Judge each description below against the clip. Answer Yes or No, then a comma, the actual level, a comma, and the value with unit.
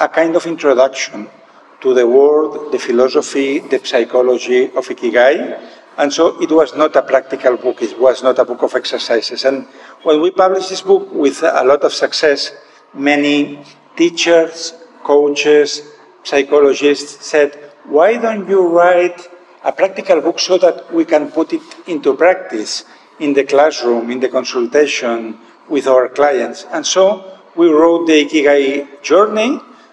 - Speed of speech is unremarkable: Yes, average, 150 wpm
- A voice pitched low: No, medium, 155 Hz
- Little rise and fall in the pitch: No, average, 5.1 semitones